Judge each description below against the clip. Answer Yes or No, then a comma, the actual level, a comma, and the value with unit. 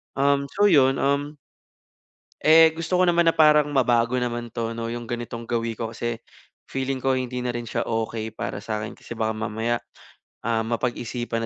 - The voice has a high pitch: No, low, 120 Hz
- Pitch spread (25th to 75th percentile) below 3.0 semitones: No, average, 3.3 semitones